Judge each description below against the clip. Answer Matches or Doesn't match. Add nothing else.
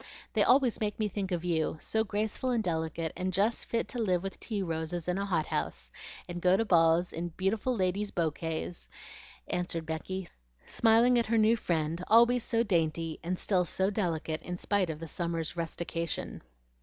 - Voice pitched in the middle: Matches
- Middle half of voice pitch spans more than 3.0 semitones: Matches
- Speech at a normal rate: Matches